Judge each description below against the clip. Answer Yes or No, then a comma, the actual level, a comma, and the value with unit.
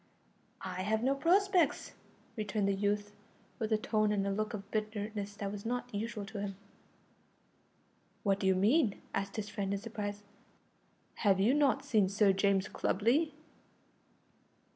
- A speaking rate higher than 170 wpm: No, average, 145 wpm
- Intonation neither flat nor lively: No, narrow, 2.3 semitones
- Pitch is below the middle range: No, high, 210 Hz